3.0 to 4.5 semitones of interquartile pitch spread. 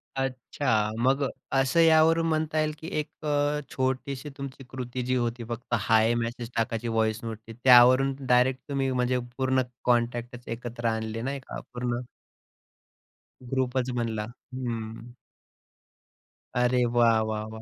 No: narrow, 2.4 semitones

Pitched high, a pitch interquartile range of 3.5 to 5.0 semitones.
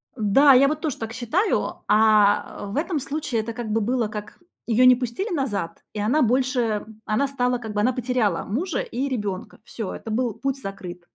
Yes: high, 240 Hz; average, 4.1 semitones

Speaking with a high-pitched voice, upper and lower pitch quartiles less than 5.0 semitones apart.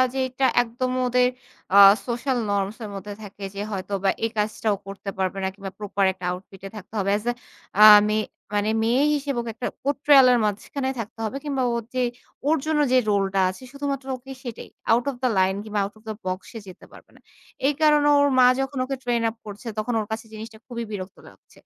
Yes: high, 225 Hz; average, 4.5 semitones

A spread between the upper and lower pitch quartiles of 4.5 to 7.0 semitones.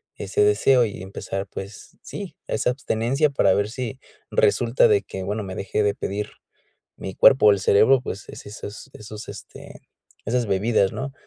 Yes: average, 5.1 semitones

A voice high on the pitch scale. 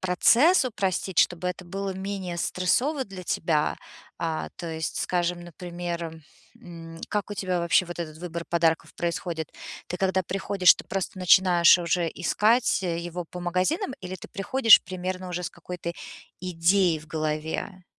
No: medium, 180 Hz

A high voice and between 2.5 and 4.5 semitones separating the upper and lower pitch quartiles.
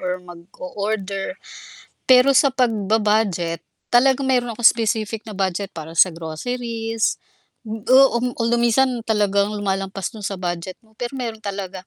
Yes: high, 215 Hz; average, 3.6 semitones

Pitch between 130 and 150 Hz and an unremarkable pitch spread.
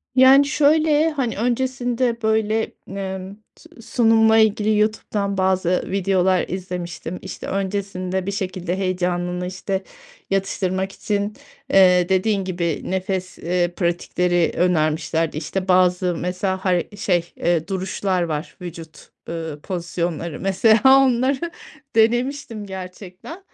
No: high, 190 Hz; average, 3.4 semitones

